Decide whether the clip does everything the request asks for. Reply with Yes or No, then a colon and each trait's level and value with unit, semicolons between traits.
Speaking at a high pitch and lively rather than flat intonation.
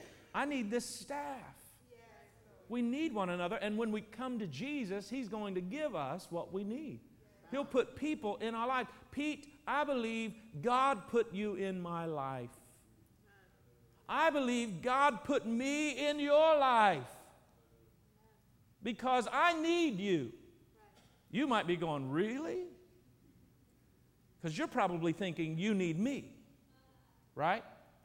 Yes: high, 230 Hz; wide, 7.2 semitones